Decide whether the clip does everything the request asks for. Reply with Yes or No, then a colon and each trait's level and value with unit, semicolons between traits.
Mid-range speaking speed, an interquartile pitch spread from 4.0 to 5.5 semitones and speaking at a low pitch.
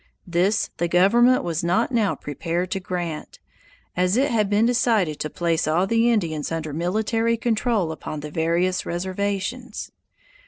No: average, 150 wpm; average, 5.0 semitones; medium, 185 Hz